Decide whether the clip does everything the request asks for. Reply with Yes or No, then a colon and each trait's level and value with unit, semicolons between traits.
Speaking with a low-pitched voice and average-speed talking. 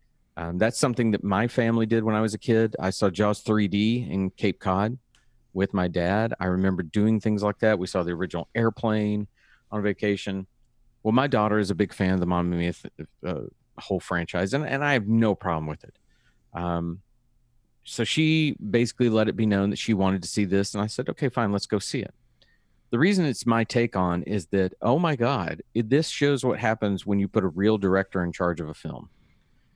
No: low, 105 Hz; fast, 215 wpm